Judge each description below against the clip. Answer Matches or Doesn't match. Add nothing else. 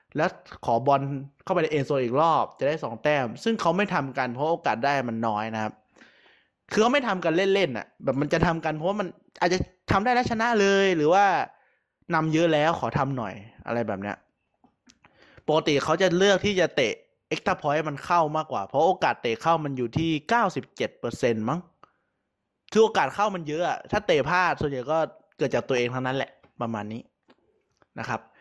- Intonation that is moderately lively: Doesn't match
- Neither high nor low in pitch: Matches